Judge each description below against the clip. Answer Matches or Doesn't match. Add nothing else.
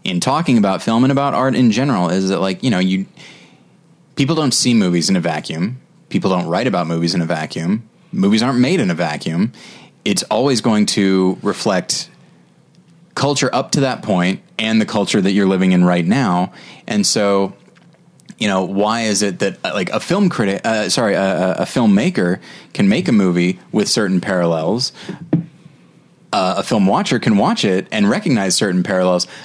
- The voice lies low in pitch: Matches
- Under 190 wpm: Doesn't match